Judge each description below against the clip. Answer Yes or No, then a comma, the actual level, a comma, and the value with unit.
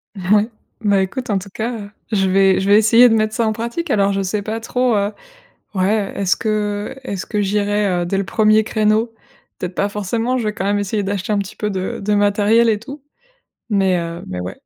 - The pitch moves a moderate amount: No, narrow, 2.0 semitones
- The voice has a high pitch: Yes, high, 205 Hz